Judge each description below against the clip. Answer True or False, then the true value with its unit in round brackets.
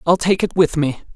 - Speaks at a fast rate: True (260 wpm)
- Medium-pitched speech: True (165 Hz)